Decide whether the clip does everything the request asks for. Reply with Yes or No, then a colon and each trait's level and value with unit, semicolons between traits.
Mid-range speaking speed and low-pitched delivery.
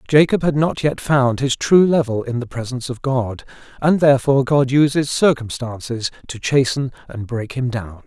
Yes: average, 180 wpm; low, 130 Hz